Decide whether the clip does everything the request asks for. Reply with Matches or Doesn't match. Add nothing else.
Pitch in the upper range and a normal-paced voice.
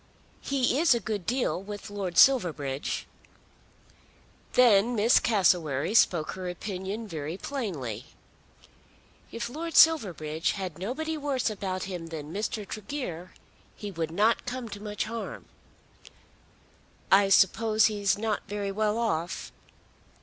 Doesn't match